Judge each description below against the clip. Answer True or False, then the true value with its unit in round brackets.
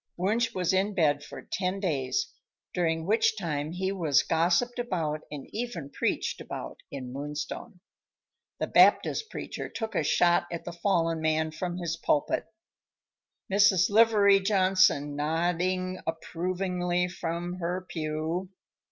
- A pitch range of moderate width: True (3.1 semitones)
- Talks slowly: True (130 wpm)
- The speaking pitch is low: False (175 Hz)